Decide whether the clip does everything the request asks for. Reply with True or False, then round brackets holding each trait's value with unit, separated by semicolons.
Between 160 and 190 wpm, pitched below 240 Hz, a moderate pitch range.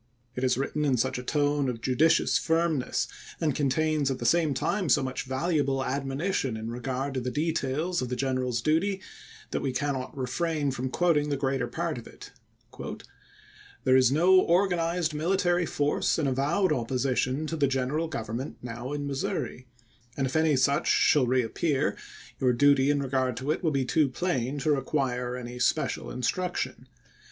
True (170 wpm; 140 Hz; 3.4 semitones)